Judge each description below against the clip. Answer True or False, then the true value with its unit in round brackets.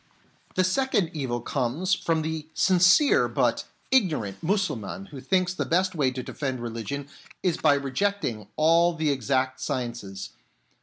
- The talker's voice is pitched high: False (150 Hz)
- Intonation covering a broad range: True (6.2 semitones)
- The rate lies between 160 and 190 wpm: False (140 wpm)